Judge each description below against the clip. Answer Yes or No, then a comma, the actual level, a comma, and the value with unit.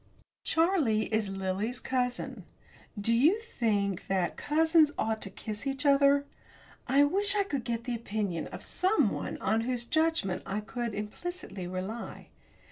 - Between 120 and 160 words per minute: Yes, average, 140 wpm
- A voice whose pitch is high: Yes, high, 240 Hz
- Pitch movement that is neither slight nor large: No, wide, 6.0 semitones